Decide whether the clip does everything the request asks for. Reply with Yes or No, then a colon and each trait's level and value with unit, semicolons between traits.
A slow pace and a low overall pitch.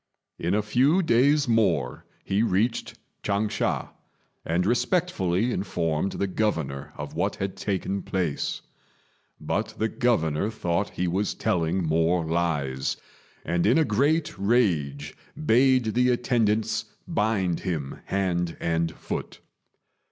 Yes: slow, 120 wpm; very low, 95 Hz